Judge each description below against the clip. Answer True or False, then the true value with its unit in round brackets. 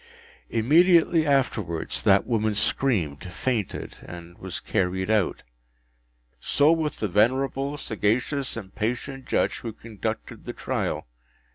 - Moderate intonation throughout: False (5.7 semitones)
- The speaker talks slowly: True (115 wpm)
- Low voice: True (115 Hz)